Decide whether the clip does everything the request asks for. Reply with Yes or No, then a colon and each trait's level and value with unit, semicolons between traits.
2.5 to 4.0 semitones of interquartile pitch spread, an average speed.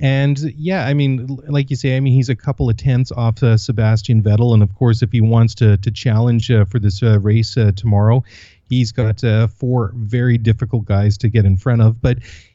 No: average, 2.8 semitones; fast, 225 wpm